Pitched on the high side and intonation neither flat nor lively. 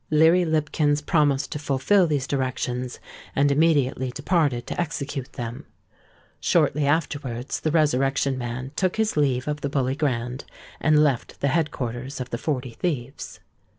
No: medium, 140 Hz; average, 3.0 semitones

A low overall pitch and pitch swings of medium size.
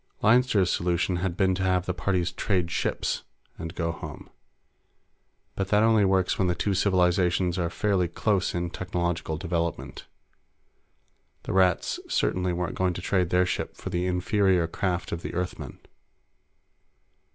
No: very low, 90 Hz; narrow, 1.5 semitones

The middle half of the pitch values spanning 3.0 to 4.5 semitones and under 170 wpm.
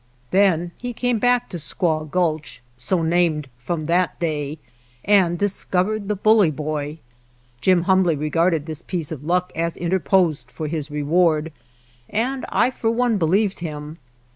Yes: average, 3.8 semitones; average, 145 wpm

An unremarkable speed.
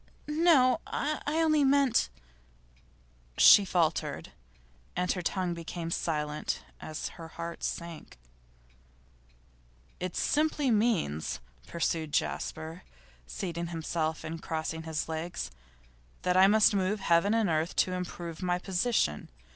No: slow, 115 wpm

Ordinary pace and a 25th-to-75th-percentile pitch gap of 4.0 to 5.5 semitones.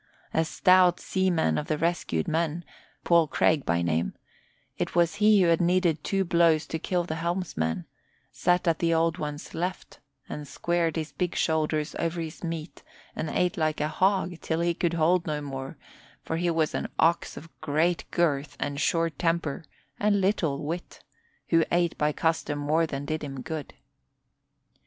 No: average, 170 wpm; narrow, 2.4 semitones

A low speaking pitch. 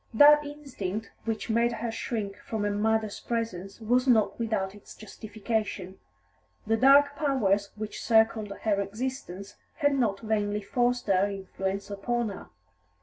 No: high, 220 Hz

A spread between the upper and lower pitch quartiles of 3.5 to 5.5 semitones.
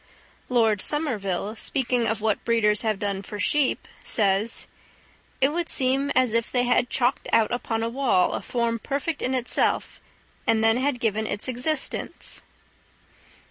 No: average, 3.1 semitones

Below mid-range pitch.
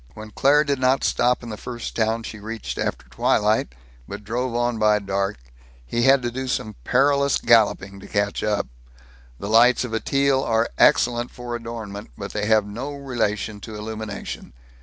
Yes: low, 115 Hz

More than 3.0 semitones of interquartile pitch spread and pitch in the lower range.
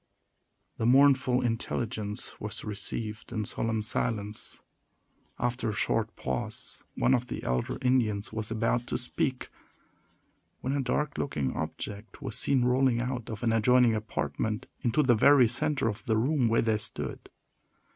No: average, 2.7 semitones; low, 115 Hz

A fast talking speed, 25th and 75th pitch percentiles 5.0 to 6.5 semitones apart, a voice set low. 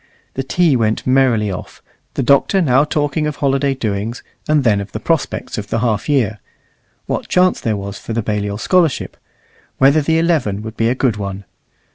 No: average, 185 wpm; wide, 5.5 semitones; low, 125 Hz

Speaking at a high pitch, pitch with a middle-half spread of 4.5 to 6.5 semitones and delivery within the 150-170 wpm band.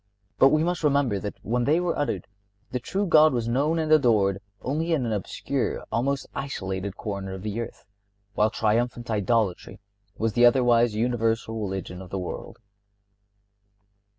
No: low, 115 Hz; average, 5.2 semitones; average, 155 wpm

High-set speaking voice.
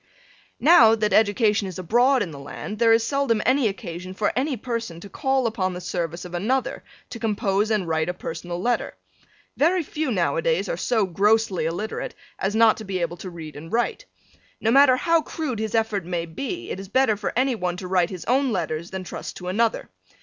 Yes: high, 215 Hz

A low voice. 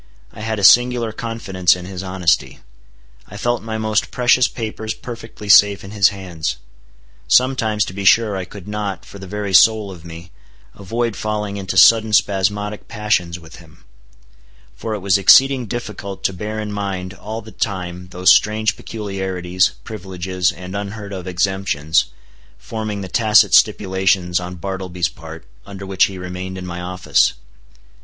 Yes: low, 100 Hz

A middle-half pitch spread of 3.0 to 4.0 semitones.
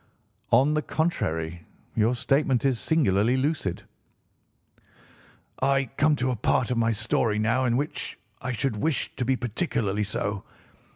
No: average, 4.4 semitones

